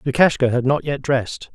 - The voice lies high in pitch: No, low, 135 Hz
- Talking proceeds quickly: No, average, 195 wpm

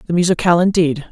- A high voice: No, medium, 170 Hz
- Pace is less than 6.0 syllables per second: No, 7.4 syllables/s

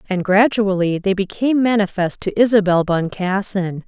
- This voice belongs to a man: No, female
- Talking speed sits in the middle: No, slow, 125 wpm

